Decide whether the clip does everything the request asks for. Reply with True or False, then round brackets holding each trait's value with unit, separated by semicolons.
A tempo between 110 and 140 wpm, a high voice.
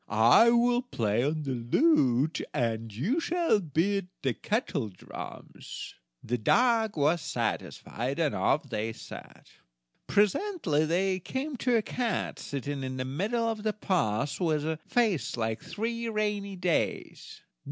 False (135 wpm; 170 Hz)